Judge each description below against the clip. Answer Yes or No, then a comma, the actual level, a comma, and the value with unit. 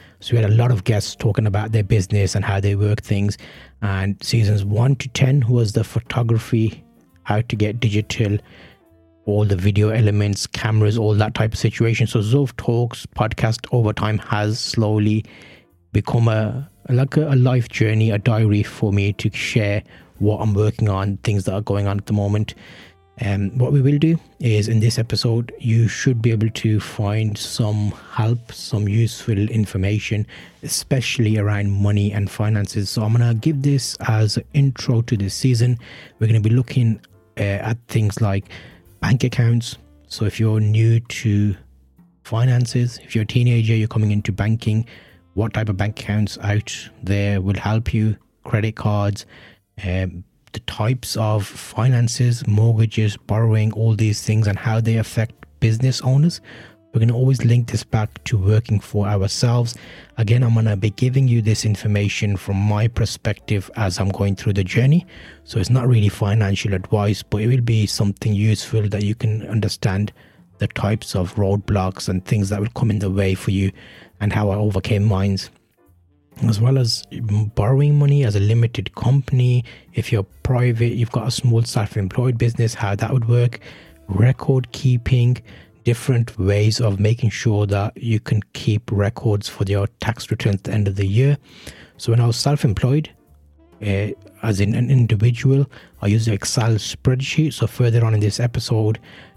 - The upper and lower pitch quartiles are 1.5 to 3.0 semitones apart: Yes, narrow, 2.6 semitones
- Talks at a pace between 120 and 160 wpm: No, average, 175 wpm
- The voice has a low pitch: Yes, low, 110 Hz